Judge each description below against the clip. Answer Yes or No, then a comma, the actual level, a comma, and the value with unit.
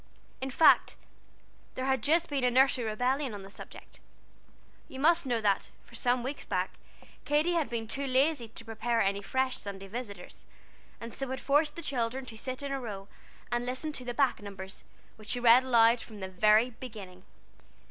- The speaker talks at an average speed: Yes, average, 190 wpm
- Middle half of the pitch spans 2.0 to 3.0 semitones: No, average, 3.6 semitones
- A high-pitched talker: Yes, high, 245 Hz